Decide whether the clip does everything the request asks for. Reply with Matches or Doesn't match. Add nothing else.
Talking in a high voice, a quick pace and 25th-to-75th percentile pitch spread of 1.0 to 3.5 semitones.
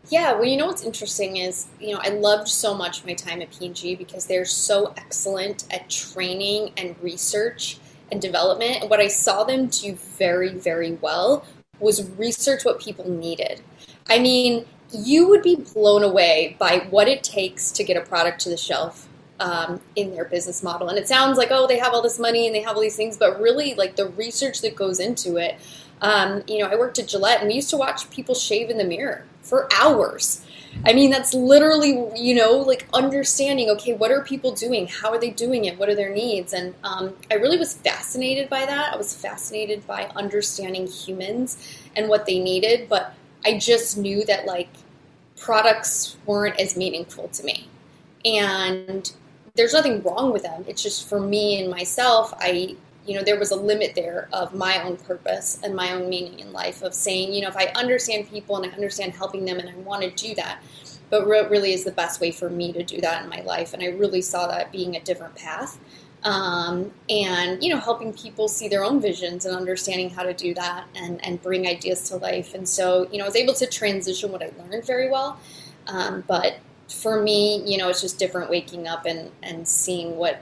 Doesn't match